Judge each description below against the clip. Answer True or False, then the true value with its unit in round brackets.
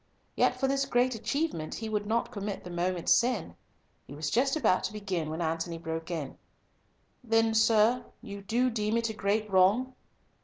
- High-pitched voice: True (210 Hz)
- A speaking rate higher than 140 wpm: True (180 wpm)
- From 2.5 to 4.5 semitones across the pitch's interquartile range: False (4.9 semitones)